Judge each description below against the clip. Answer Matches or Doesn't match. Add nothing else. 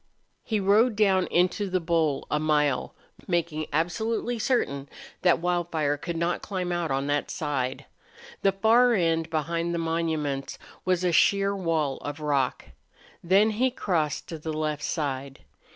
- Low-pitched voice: Doesn't match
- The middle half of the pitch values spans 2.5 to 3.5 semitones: Doesn't match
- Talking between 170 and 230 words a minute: Doesn't match